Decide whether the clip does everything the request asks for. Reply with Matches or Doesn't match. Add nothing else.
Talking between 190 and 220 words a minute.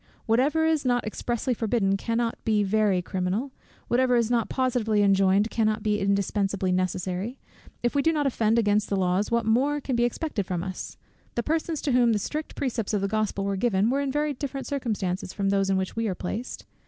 Matches